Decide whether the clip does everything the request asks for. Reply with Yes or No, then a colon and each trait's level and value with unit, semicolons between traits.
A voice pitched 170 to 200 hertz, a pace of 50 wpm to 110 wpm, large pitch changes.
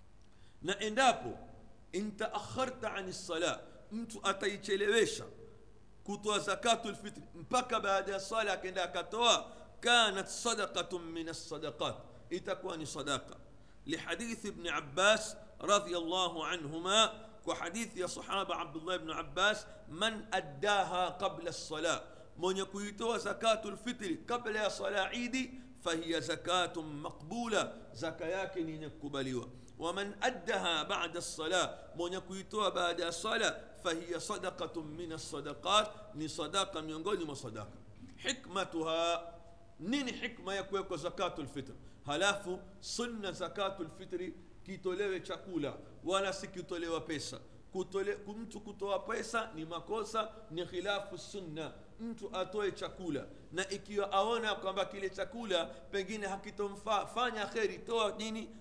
No: high, 190 Hz; average, 105 wpm; average, 4.0 semitones